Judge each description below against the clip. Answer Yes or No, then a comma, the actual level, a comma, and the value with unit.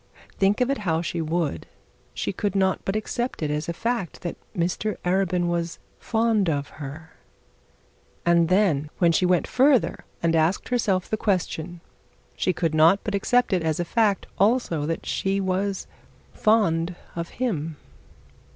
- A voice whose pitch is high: No, medium, 180 Hz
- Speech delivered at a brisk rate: No, average, 160 wpm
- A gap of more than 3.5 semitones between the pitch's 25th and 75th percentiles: Yes, average, 3.9 semitones